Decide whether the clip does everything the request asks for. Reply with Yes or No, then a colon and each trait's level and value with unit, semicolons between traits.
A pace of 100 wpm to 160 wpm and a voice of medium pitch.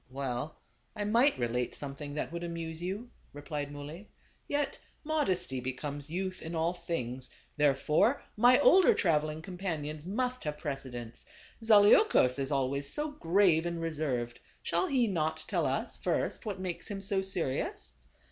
Yes: average, 155 wpm; medium, 160 Hz